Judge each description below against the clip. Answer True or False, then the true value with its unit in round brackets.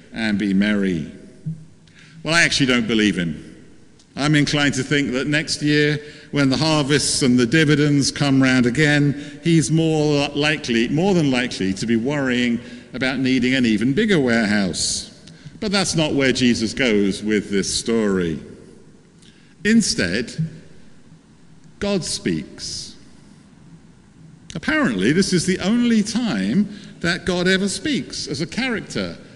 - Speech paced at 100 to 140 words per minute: True (135 wpm)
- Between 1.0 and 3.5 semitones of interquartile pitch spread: False (5.1 semitones)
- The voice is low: False (145 Hz)